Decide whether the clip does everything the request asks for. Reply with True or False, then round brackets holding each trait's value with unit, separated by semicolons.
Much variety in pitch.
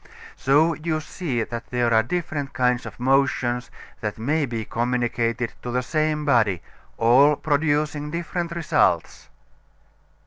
False (4.2 semitones)